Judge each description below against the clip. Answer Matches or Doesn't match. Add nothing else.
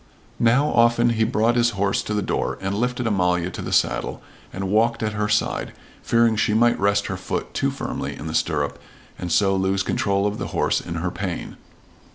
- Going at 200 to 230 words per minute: Matches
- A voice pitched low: Matches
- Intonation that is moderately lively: Matches